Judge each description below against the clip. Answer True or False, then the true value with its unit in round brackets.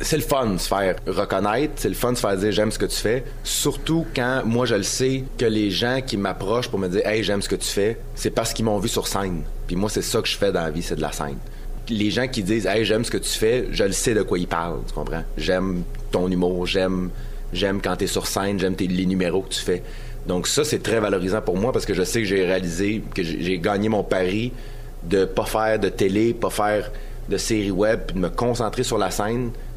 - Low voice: True (105 Hz)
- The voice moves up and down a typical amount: True (3.7 semitones)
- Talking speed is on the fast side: True (265 wpm)